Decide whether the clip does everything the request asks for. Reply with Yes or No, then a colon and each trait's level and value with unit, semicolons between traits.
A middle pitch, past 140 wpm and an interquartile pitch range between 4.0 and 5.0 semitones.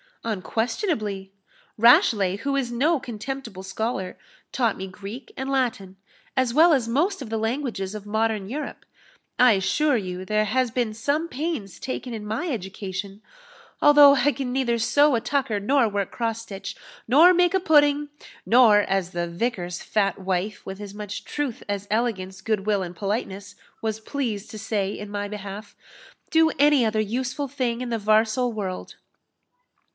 No: high, 225 Hz; average, 160 wpm; average, 4.7 semitones